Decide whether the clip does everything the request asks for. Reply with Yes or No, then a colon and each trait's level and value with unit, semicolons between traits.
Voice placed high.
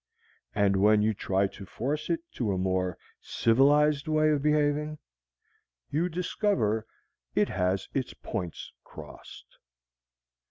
No: low, 125 Hz